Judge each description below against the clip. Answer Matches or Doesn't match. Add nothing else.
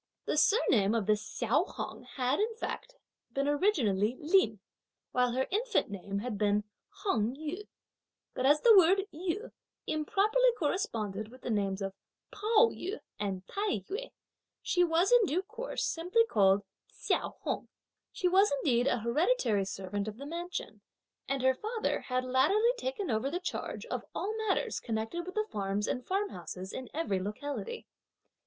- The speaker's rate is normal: Matches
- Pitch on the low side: Doesn't match